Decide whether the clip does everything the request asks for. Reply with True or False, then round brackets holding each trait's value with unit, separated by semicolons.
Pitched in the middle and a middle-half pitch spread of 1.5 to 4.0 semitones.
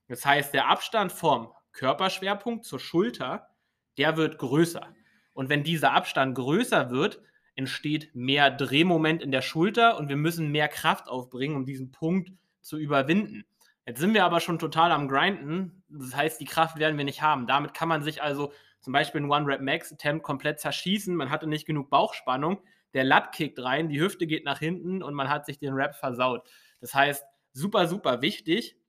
True (150 Hz; 3.5 semitones)